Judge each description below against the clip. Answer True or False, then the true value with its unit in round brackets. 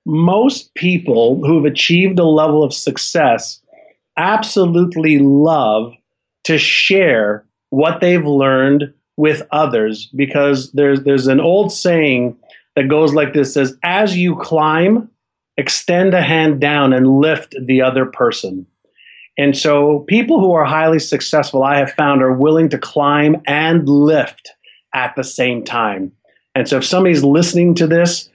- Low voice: False (150 Hz)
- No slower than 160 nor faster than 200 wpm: False (140 wpm)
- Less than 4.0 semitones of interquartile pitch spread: True (3.5 semitones)